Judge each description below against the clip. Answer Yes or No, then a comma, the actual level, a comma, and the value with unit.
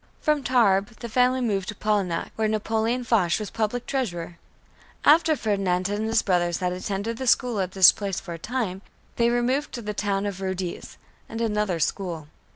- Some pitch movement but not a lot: Yes, average, 4.0 semitones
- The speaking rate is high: No, average, 180 wpm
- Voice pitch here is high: Yes, high, 210 Hz